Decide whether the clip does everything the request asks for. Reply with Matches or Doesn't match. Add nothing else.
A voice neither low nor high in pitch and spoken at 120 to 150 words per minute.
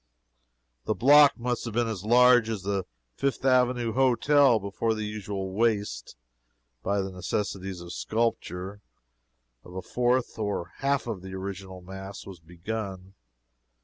Doesn't match